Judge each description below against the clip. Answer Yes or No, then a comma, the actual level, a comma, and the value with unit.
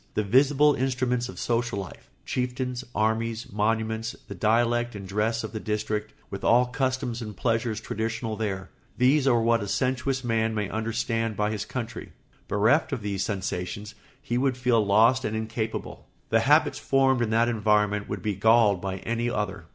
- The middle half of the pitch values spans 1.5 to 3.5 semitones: Yes, narrow, 2.5 semitones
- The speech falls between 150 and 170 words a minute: Yes, average, 165 wpm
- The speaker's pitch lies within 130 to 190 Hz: No, low, 115 Hz